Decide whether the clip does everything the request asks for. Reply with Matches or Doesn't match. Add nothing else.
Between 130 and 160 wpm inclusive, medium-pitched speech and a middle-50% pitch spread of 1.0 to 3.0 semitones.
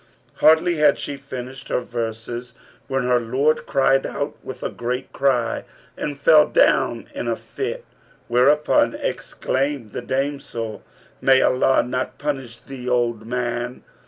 Doesn't match